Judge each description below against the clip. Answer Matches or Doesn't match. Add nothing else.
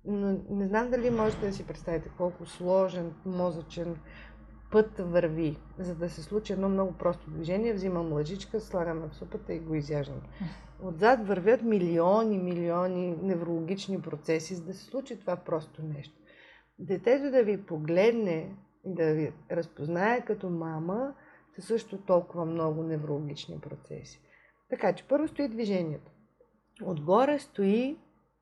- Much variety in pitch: Doesn't match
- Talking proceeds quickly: Doesn't match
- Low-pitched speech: Doesn't match